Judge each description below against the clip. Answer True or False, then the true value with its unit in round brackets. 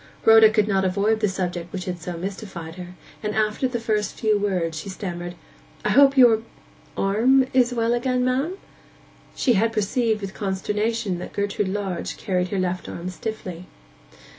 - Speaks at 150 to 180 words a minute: True (165 wpm)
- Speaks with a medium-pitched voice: False (205 Hz)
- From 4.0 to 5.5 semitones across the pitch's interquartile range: False (3.6 semitones)